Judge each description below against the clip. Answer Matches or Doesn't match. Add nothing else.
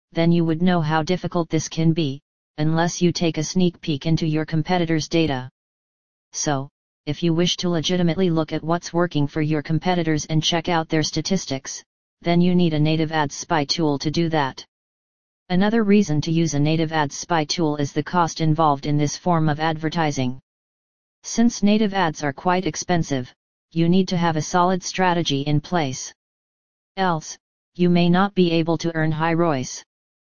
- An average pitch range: Doesn't match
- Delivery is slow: Doesn't match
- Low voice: Doesn't match